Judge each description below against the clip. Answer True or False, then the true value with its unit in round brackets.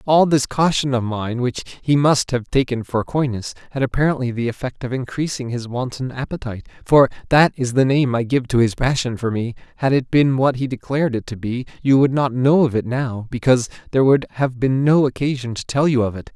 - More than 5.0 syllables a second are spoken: True (5.6 syllables/s)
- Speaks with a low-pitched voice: True (130 Hz)